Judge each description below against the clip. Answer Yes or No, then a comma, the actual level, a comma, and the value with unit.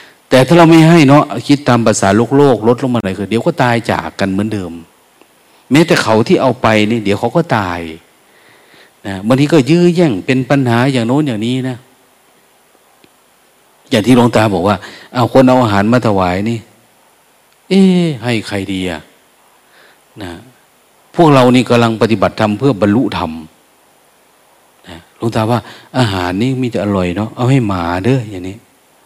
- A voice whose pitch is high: No, low, 120 Hz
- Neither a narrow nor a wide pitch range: Yes, average, 4.5 semitones